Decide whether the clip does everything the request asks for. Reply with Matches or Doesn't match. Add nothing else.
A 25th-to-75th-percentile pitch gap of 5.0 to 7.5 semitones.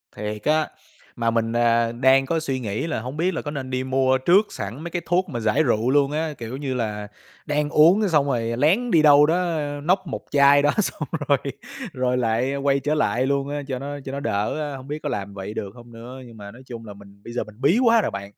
Doesn't match